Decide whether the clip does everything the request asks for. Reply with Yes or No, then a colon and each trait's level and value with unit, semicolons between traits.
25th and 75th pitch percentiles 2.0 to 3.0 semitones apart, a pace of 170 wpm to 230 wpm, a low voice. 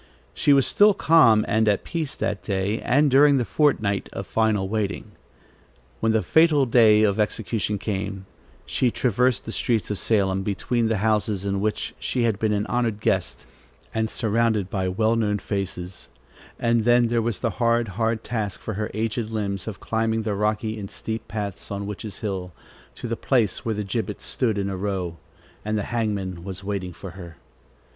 Yes: narrow, 2.6 semitones; average, 180 wpm; low, 110 Hz